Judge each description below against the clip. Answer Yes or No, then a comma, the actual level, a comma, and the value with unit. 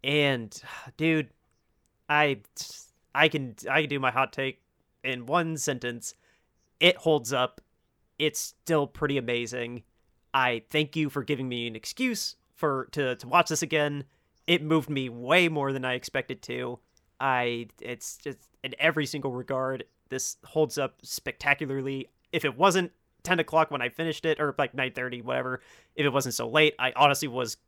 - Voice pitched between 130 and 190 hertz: Yes, low, 135 Hz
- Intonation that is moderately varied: Yes, average, 3.6 semitones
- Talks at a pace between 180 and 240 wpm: No, average, 165 wpm